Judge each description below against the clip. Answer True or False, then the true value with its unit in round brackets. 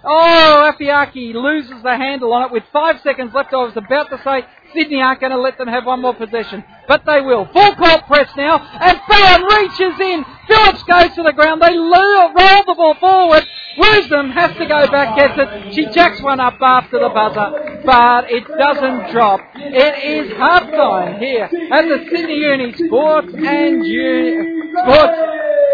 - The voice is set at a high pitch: True (295 Hz)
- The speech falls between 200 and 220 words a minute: False (180 wpm)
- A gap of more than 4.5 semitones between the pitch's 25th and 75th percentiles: False (4.2 semitones)